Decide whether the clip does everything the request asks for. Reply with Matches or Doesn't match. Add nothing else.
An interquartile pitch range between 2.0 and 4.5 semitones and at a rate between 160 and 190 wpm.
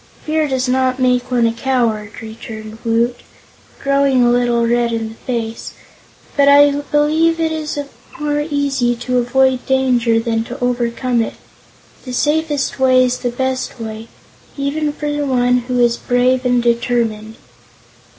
Doesn't match